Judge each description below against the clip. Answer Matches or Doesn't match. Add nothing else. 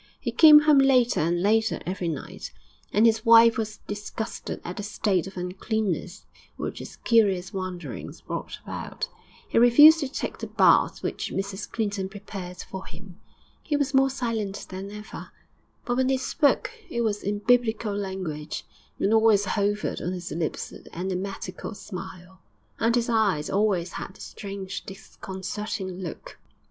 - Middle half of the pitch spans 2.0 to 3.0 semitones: Doesn't match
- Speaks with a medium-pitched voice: Doesn't match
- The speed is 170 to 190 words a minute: Doesn't match